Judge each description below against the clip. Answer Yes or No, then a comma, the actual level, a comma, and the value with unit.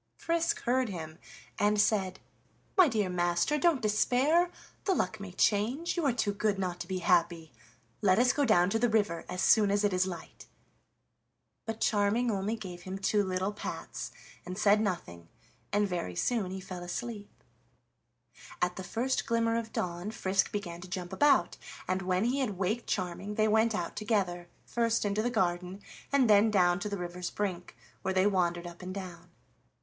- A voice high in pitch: Yes, high, 200 Hz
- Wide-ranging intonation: No, average, 3.7 semitones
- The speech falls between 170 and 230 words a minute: Yes, average, 180 wpm